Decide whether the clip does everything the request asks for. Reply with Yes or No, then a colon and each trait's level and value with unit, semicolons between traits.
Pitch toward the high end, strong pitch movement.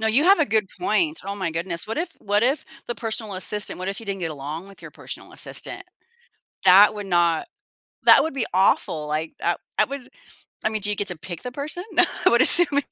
Yes: high, 205 Hz; wide, 6.4 semitones